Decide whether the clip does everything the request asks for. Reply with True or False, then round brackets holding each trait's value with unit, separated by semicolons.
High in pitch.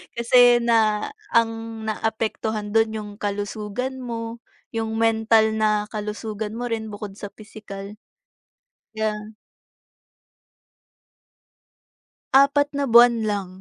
True (220 Hz)